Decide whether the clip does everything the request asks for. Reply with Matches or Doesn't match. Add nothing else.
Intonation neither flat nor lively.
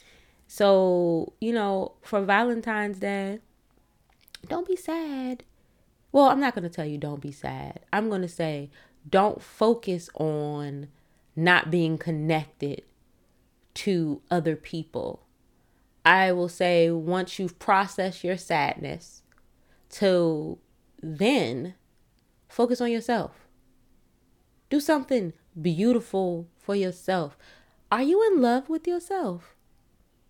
Doesn't match